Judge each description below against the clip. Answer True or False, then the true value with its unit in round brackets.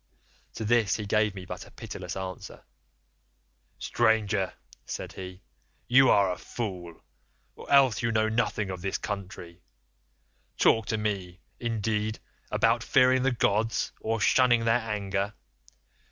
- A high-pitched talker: False (105 Hz)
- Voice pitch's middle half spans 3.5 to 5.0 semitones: False (2.9 semitones)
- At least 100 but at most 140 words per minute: True (135 wpm)